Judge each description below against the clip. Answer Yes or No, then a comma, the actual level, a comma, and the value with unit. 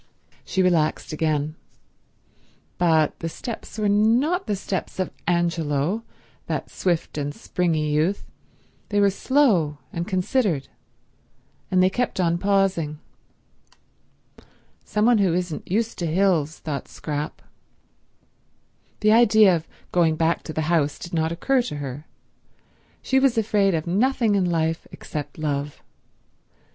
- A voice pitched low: No, medium, 175 Hz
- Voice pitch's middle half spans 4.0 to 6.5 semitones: Yes, average, 4.7 semitones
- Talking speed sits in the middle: No, slow, 130 wpm